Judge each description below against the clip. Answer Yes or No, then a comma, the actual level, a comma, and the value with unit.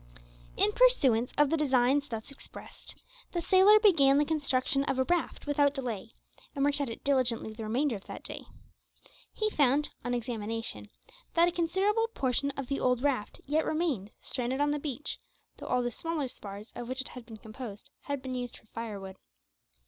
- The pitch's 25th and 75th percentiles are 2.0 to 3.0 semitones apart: No, average, 3.9 semitones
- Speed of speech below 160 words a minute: No, average, 185 wpm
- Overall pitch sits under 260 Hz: No, very high, 270 Hz